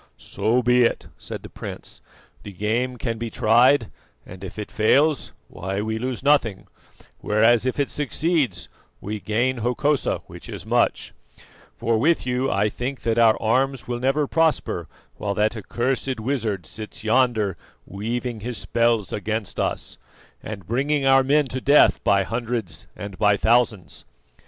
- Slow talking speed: No, average, 150 wpm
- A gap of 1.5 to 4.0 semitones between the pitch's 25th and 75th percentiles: Yes, average, 3.3 semitones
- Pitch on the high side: No, low, 115 Hz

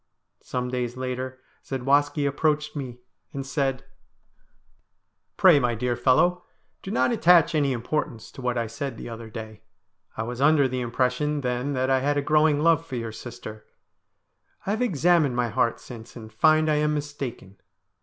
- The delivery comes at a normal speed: Yes, average, 170 wpm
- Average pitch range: Yes, average, 3.7 semitones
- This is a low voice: Yes, low, 130 Hz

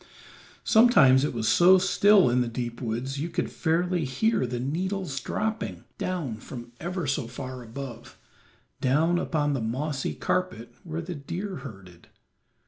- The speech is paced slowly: No, average, 145 wpm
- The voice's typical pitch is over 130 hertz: Yes, medium, 140 Hz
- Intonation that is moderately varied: No, wide, 6.4 semitones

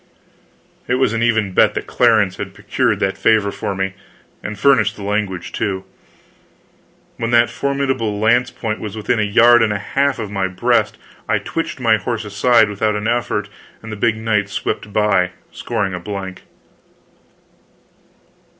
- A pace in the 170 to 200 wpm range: No, average, 160 wpm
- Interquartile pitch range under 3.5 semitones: Yes, average, 2.7 semitones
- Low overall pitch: Yes, low, 105 Hz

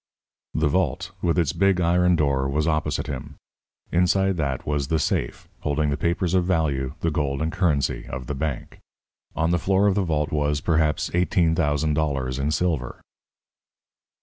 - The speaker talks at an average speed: Yes, average, 170 wpm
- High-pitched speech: No, very low, 75 Hz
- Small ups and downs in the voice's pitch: No, average, 3.3 semitones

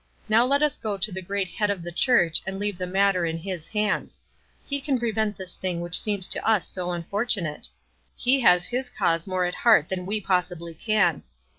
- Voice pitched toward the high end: Yes, high, 195 Hz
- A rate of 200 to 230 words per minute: Yes, fast, 205 wpm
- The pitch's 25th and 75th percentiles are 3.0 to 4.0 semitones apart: Yes, average, 3.5 semitones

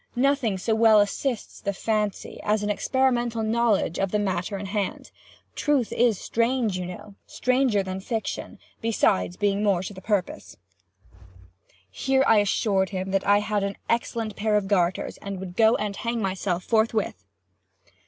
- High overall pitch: Yes, high, 210 Hz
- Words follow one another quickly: No, average, 155 wpm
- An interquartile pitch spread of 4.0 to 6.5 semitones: No, average, 3.0 semitones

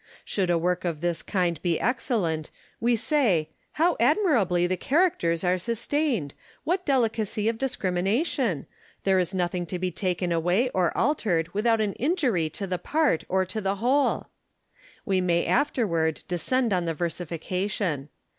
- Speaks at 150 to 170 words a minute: Yes, average, 155 wpm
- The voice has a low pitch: No, high, 190 Hz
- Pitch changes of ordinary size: No, wide, 5.7 semitones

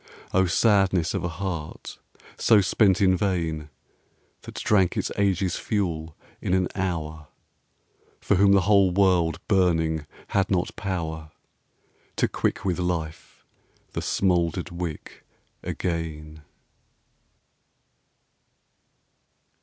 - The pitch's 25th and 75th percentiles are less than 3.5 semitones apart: Yes, average, 2.9 semitones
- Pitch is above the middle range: No, very low, 90 Hz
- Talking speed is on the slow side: Yes, slow, 105 wpm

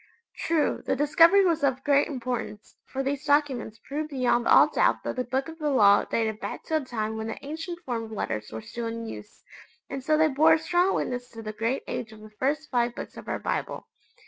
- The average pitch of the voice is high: Yes, very high, 260 Hz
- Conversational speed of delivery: No, fast, 225 wpm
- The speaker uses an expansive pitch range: No, average, 5.0 semitones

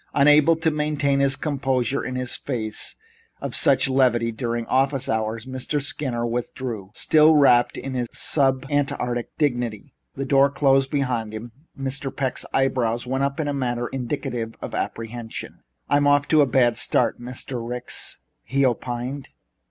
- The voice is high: No, low, 130 Hz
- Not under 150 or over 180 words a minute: Yes, average, 155 wpm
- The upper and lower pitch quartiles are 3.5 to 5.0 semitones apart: No, average, 2.7 semitones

